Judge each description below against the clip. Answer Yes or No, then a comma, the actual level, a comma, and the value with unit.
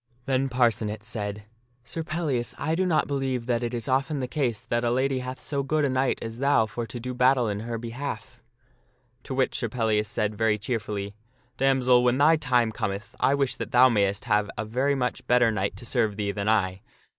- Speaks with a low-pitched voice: Yes, low, 120 Hz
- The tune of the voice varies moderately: Yes, average, 3.4 semitones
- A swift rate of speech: Yes, fast, 215 wpm